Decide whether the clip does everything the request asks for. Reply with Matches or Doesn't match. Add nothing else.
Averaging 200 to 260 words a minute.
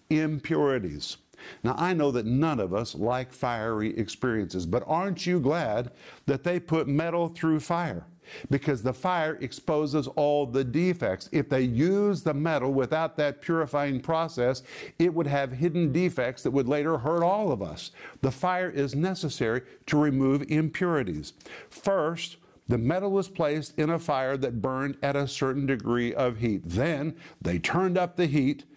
Doesn't match